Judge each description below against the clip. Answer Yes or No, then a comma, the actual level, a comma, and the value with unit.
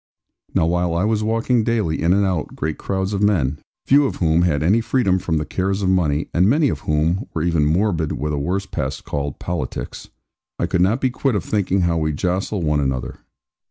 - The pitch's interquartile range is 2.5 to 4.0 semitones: No, average, 4.6 semitones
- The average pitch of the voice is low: Yes, very low, 90 Hz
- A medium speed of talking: No, fast, 215 wpm